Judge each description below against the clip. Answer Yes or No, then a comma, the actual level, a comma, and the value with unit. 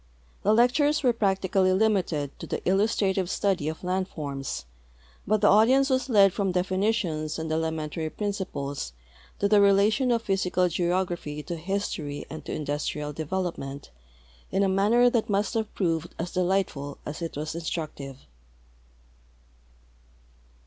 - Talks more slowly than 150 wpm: Yes, average, 140 wpm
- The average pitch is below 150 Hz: No, medium, 185 Hz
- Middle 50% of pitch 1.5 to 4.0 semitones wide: No, average, 4.6 semitones